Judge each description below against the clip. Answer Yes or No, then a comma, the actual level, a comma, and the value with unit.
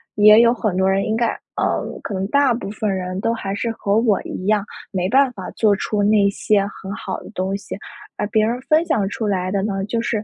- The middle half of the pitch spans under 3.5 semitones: Yes, narrow, 2.6 semitones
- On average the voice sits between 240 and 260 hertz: No, high, 205 Hz